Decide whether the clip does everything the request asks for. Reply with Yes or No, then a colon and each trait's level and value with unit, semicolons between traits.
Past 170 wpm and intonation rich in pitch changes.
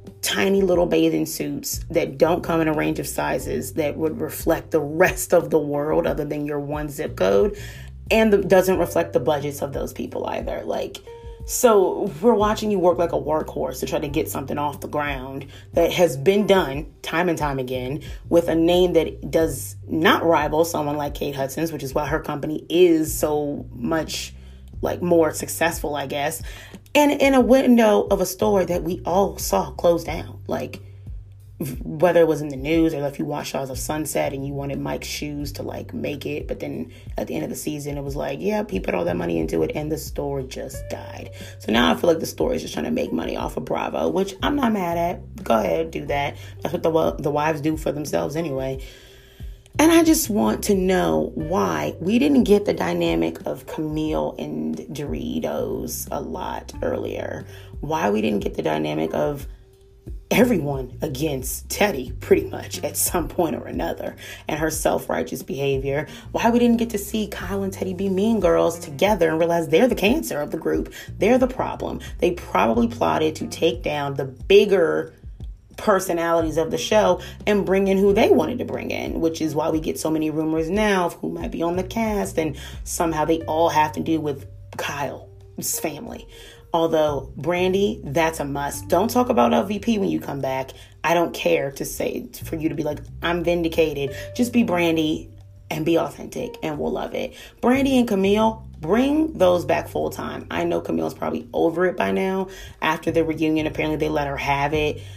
Yes: average, 200 wpm; wide, 6.0 semitones